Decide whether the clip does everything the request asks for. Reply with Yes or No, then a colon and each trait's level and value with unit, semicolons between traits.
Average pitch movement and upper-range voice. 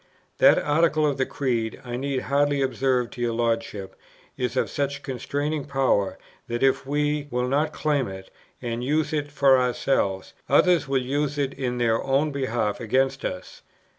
No: average, 3.0 semitones; low, 135 Hz